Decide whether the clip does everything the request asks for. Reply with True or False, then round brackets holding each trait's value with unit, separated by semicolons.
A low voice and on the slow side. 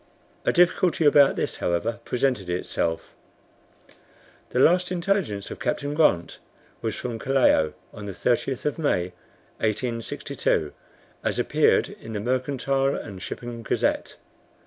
True (120 Hz; 125 wpm)